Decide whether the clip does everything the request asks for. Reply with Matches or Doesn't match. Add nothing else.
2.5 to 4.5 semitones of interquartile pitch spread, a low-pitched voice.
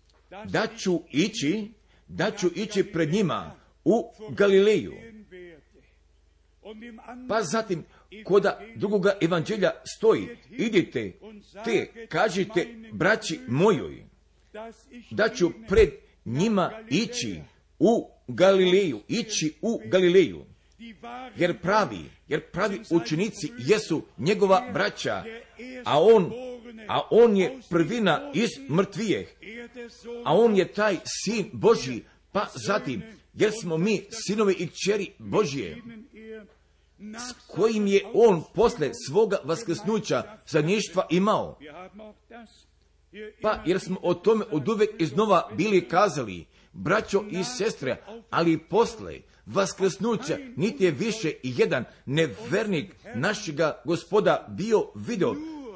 Doesn't match